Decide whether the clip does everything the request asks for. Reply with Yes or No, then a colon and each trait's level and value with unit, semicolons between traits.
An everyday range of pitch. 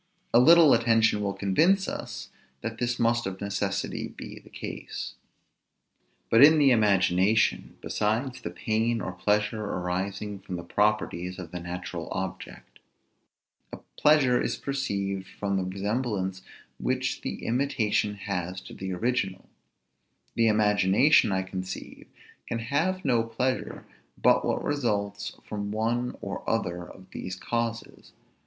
Yes: average, 3.8 semitones